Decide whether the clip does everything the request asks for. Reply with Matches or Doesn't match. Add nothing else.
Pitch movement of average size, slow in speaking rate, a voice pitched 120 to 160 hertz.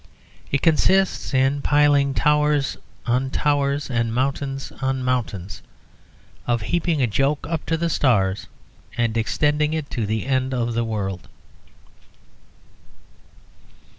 Matches